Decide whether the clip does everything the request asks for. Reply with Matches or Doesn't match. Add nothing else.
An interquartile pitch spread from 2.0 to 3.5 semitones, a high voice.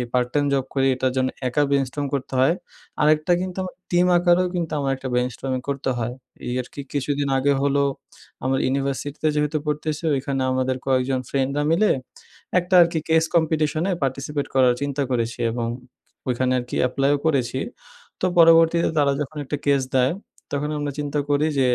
Doesn't match